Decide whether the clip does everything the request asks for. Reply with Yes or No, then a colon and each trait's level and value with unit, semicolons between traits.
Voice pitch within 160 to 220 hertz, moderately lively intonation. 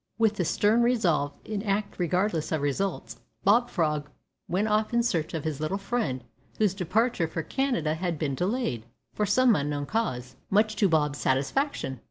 No: medium, 185 Hz; wide, 6.3 semitones